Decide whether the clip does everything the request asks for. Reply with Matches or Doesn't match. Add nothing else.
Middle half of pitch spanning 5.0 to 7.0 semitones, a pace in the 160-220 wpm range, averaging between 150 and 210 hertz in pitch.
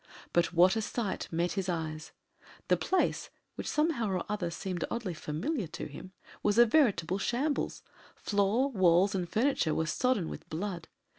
Matches